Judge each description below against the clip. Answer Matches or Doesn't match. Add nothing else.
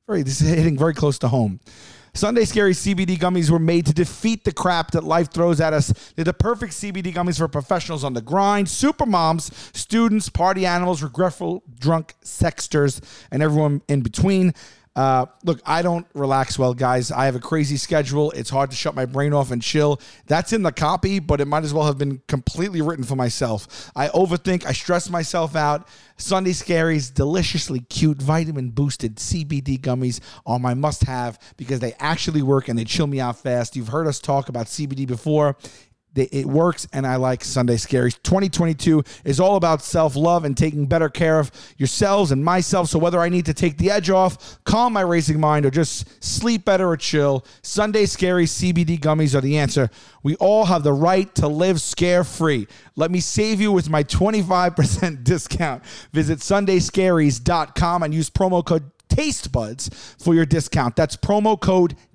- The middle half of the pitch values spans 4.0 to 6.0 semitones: Matches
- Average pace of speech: Matches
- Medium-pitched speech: Matches